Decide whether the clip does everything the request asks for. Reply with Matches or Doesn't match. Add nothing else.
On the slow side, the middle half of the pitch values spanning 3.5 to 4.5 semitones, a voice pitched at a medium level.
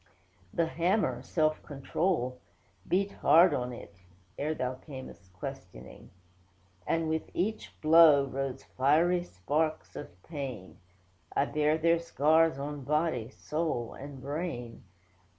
Matches